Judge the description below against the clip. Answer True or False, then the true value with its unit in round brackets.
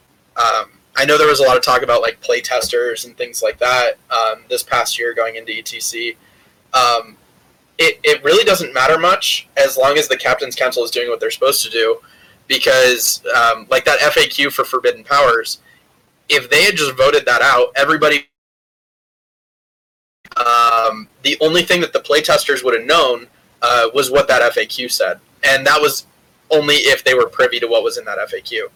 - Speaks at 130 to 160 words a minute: False (190 wpm)